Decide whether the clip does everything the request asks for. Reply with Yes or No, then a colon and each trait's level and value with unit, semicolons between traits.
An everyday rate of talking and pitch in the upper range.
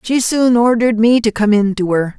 No: fast, 245 wpm; high, 225 Hz